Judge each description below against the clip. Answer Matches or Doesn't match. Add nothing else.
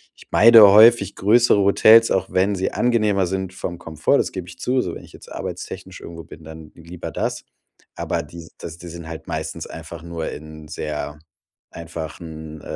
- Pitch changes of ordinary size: Matches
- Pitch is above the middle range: Doesn't match